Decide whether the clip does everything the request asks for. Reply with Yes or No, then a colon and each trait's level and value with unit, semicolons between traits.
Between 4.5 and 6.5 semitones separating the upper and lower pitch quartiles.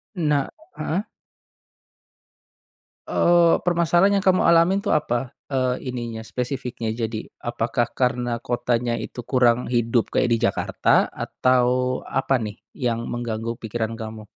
No: average, 2.8 semitones